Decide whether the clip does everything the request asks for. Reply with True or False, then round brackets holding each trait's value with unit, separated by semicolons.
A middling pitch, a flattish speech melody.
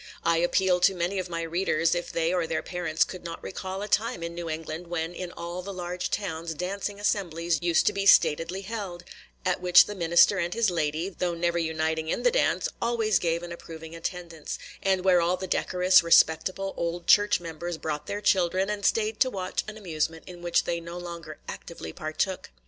True (175 Hz; 2.2 semitones)